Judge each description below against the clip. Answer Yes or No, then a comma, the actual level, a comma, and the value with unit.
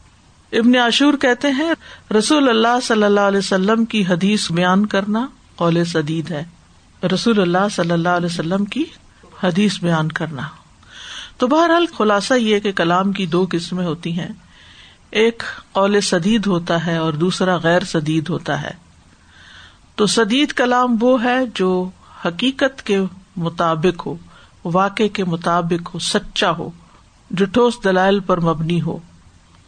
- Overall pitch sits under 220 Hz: Yes, high, 190 Hz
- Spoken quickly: No, average, 140 wpm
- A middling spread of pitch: Yes, average, 4.7 semitones